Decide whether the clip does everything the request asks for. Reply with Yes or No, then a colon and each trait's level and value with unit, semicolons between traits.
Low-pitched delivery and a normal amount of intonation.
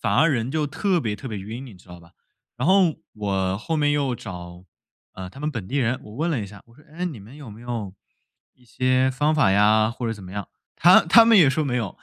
No: low, 120 Hz; wide, 6.4 semitones